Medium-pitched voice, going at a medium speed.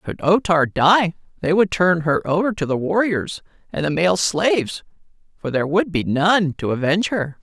Yes: medium, 170 Hz; average, 195 wpm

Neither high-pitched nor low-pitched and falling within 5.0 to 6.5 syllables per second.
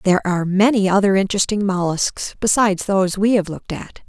No: high, 195 Hz; 6.2 syllables/s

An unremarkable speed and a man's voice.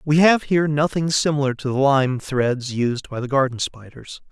Yes: average, 195 wpm; male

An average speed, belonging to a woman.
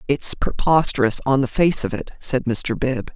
Yes: average, 190 wpm; female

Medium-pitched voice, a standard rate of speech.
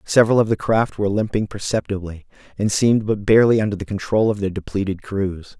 No: low, 105 Hz; average, 195 wpm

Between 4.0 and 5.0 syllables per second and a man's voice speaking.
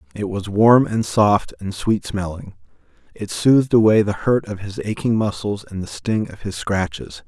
Yes: 4.6 syllables/s; male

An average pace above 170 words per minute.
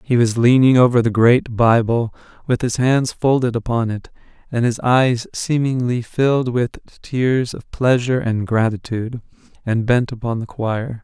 No: average, 160 wpm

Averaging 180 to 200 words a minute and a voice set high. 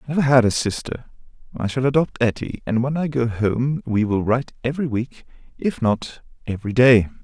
No: average, 190 wpm; low, 125 Hz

